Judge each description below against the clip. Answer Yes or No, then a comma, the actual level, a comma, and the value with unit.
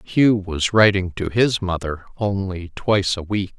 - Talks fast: No, average, 165 wpm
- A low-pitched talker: Yes, very low, 95 Hz